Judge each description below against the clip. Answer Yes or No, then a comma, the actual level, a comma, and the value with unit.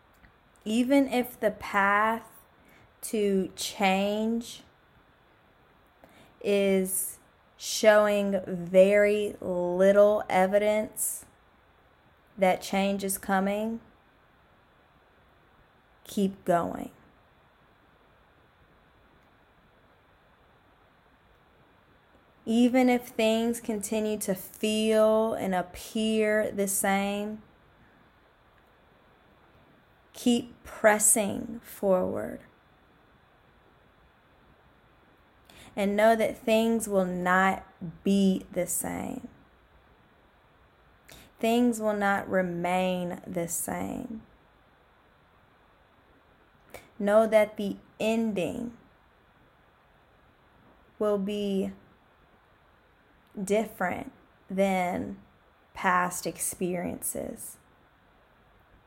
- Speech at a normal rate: No, slow, 55 wpm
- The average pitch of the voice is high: Yes, high, 205 Hz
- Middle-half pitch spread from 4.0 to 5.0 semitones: No, average, 2.7 semitones